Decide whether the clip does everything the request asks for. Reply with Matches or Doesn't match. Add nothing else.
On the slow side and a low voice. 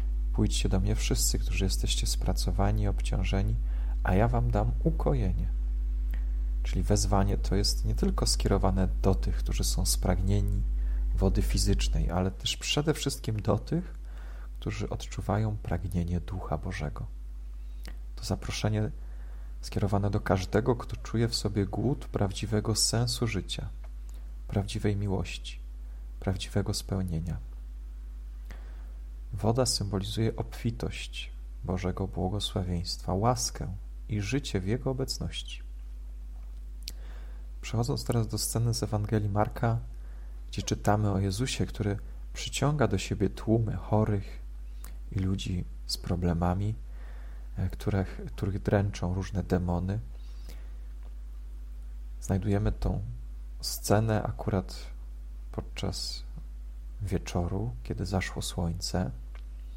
Matches